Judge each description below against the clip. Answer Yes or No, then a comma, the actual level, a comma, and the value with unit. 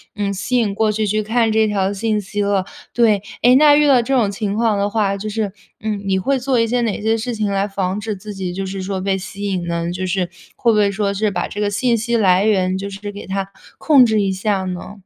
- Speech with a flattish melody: Yes, narrow, 2.3 semitones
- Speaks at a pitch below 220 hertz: Yes, high, 205 Hz